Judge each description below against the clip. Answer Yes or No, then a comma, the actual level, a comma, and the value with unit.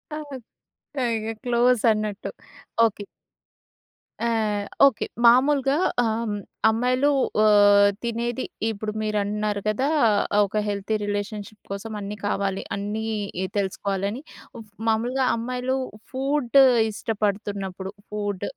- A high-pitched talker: Yes, high, 215 Hz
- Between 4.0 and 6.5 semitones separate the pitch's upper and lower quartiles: No, average, 2.8 semitones